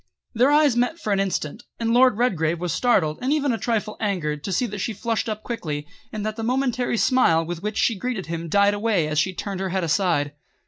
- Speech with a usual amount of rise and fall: No, wide, 5.7 semitones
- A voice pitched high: Yes, high, 205 Hz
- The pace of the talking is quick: Yes, fast, 230 wpm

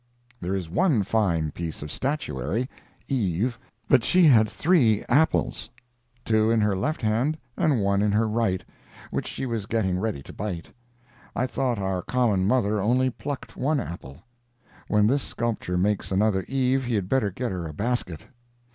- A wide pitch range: No, average, 4.8 semitones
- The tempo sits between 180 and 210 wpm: No, average, 155 wpm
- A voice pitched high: No, low, 110 Hz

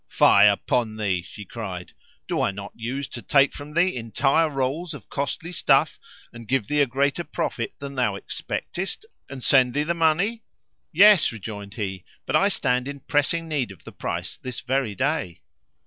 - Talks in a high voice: No, low, 135 Hz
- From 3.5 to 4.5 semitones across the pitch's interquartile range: No, average, 5.3 semitones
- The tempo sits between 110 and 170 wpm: No, average, 180 wpm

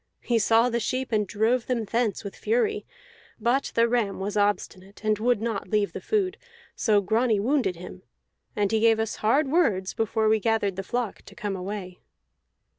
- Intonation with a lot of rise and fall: No, average, 3.0 semitones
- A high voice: Yes, high, 220 Hz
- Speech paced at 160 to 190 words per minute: Yes, average, 185 wpm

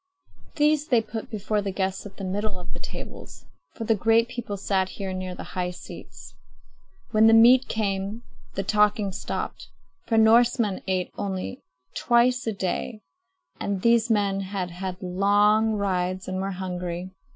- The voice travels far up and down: No, average, 3.0 semitones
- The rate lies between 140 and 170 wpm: Yes, average, 160 wpm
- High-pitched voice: Yes, high, 200 Hz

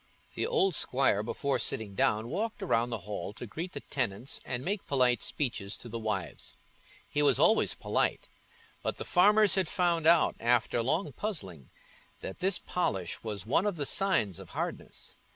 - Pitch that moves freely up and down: Yes, wide, 8.7 semitones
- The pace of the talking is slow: No, average, 170 wpm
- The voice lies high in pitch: No, low, 135 Hz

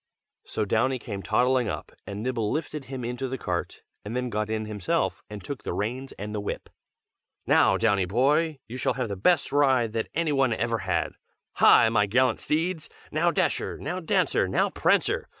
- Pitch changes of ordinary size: Yes, average, 4.3 semitones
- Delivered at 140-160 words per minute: No, average, 185 wpm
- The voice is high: No, low, 120 Hz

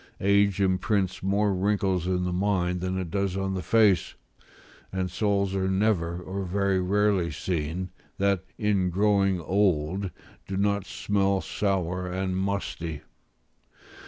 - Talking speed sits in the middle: No, slow, 130 wpm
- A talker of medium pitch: No, very low, 95 Hz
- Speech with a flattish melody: Yes, narrow, 1.6 semitones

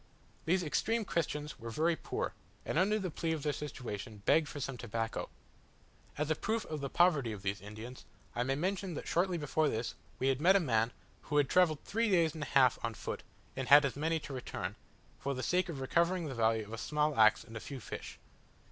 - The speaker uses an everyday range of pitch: No, wide, 5.8 semitones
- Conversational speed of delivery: No, fast, 220 wpm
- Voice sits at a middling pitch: Yes, medium, 145 Hz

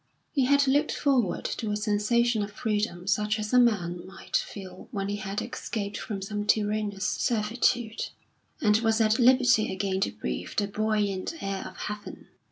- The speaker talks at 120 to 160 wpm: No, average, 170 wpm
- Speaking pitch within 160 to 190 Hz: No, high, 210 Hz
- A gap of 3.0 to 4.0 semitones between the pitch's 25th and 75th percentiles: No, narrow, 2.6 semitones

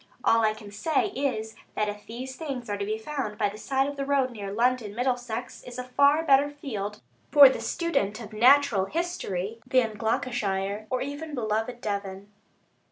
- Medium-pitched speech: No, high, 235 Hz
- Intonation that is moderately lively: Yes, average, 4.7 semitones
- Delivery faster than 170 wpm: Yes, average, 180 wpm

